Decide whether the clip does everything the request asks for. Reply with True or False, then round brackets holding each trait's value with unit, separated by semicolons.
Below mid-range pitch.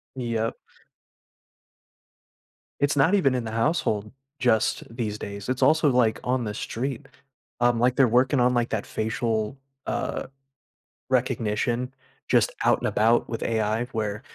True (120 Hz)